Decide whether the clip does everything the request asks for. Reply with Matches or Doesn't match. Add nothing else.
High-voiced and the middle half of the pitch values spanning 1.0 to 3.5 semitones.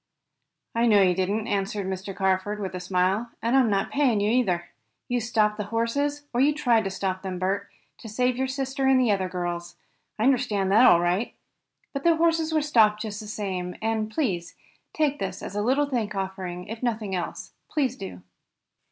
Doesn't match